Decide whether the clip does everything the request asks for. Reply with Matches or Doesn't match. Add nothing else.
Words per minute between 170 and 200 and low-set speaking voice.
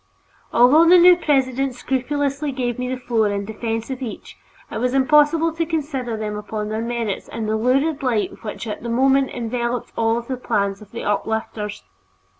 Doesn't match